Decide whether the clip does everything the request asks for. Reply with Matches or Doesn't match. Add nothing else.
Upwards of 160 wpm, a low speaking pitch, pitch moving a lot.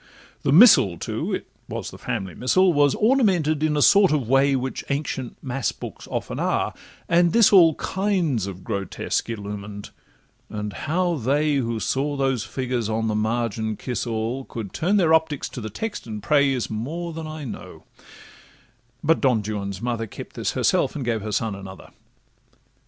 Matches